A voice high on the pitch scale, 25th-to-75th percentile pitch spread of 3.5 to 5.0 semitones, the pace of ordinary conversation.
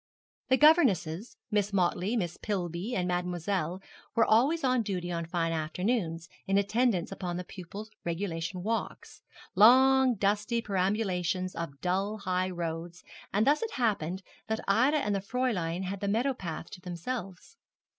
Yes: high, 195 Hz; average, 4.3 semitones; average, 145 wpm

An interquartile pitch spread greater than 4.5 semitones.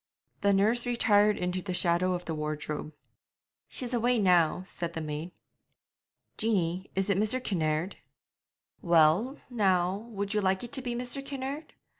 Yes: wide, 5.4 semitones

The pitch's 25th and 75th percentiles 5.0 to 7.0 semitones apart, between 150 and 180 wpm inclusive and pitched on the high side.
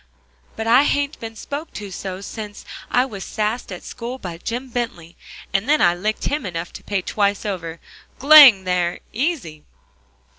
Yes: wide, 5.5 semitones; average, 170 wpm; high, 215 Hz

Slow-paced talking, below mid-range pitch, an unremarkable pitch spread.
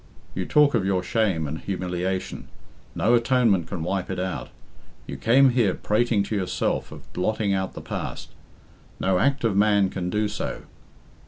No: average, 165 wpm; low, 100 Hz; average, 3.6 semitones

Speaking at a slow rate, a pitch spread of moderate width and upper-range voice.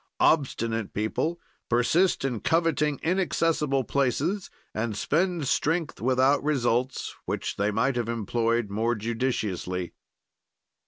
No: slow, 105 wpm; average, 5.0 semitones; low, 130 Hz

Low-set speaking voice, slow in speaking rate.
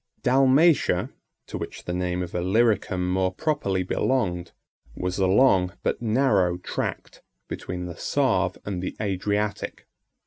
Yes: very low, 95 Hz; slow, 130 wpm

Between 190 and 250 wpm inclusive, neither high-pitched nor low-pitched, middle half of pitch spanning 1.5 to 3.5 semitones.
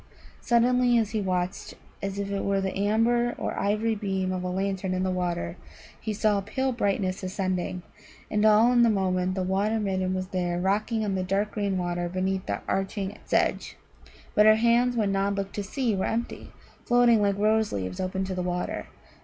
No: average, 195 wpm; high, 195 Hz; average, 2.7 semitones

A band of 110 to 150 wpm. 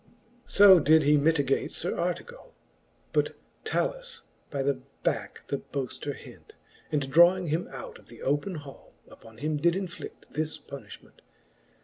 Yes: average, 145 wpm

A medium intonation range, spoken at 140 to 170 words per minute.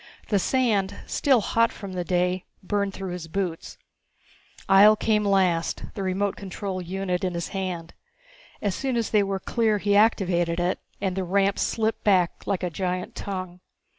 No: narrow, 2.1 semitones; average, 165 wpm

